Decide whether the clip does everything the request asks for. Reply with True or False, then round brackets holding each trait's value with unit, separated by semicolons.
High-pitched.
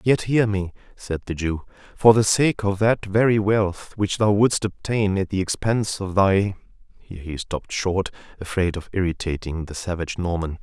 False (95 Hz)